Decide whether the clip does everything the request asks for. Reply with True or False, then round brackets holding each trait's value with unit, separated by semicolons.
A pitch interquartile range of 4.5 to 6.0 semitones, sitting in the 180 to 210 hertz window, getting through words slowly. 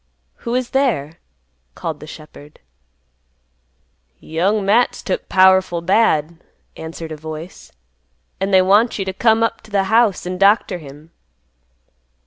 True (5.1 semitones; 190 Hz; 130 wpm)